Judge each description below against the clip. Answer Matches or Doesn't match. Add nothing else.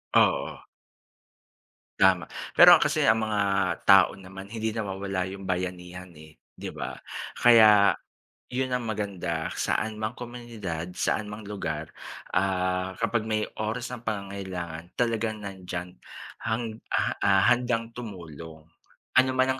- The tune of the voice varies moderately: Matches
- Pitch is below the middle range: Matches